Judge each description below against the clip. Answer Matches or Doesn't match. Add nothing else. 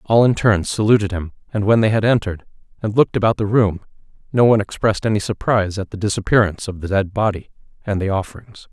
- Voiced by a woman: Doesn't match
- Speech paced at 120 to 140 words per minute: Doesn't match